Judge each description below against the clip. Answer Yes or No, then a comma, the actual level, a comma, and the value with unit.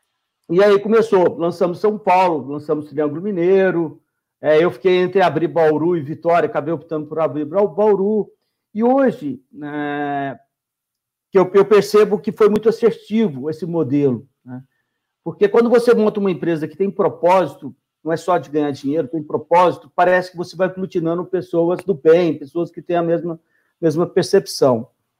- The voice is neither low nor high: Yes, medium, 170 Hz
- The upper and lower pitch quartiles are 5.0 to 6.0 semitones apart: No, average, 4.3 semitones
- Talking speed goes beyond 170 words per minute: No, average, 155 wpm